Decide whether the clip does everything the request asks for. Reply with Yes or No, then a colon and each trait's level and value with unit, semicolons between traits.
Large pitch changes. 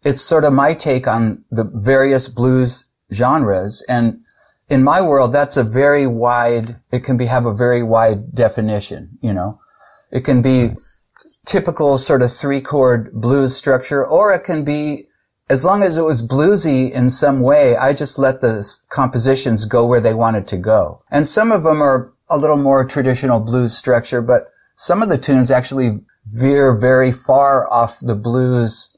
No: average, 2.8 semitones